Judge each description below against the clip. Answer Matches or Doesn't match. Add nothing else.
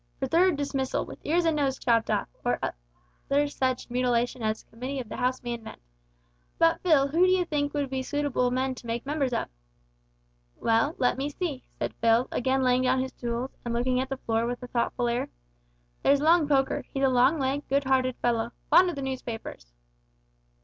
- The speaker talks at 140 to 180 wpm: Doesn't match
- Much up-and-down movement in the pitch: Doesn't match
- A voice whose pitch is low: Doesn't match